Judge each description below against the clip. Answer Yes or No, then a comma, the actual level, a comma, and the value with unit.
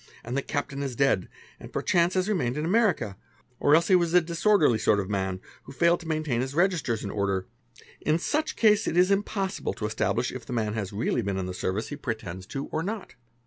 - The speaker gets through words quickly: Yes, fast, 220 wpm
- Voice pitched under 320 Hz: Yes, medium, 140 Hz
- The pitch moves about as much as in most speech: No, wide, 8.4 semitones